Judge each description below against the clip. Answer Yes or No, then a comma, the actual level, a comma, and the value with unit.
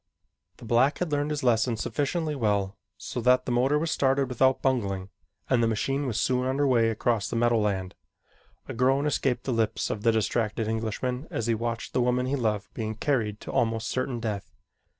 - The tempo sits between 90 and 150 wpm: No, average, 190 wpm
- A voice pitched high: No, low, 120 Hz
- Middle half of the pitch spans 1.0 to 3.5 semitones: Yes, average, 3.1 semitones